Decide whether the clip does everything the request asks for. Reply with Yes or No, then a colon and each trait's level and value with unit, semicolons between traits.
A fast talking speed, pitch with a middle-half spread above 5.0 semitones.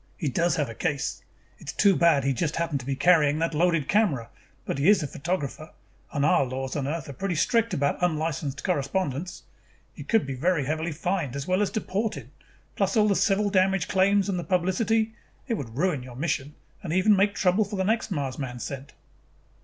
Yes: fast, 210 wpm; wide, 5.4 semitones